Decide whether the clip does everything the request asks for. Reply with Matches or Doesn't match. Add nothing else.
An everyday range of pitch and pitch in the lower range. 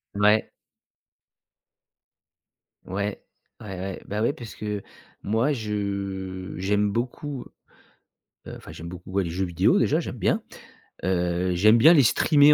Matches